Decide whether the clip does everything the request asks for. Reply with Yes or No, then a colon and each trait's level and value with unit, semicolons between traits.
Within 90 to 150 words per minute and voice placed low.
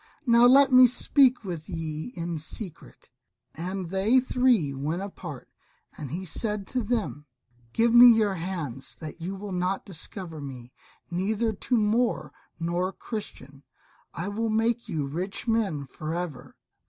No: average, 145 wpm; high, 190 Hz